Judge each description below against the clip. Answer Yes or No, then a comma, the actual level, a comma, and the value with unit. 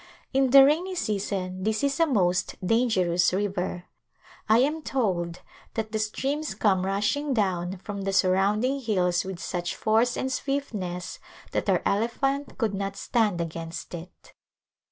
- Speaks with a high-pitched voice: Yes, high, 205 Hz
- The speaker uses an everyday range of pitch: No, wide, 5.9 semitones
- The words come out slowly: No, average, 150 wpm